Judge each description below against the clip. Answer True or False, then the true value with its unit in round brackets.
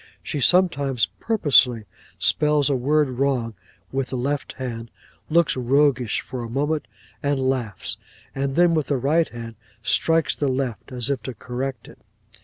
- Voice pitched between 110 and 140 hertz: True (135 Hz)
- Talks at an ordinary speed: True (155 wpm)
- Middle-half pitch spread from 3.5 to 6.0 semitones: False (3.1 semitones)